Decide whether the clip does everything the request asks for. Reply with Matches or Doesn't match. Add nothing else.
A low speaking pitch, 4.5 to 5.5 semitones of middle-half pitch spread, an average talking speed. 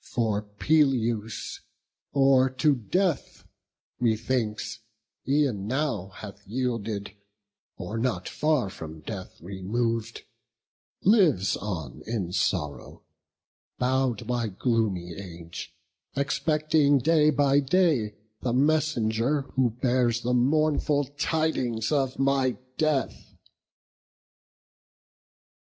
Doesn't match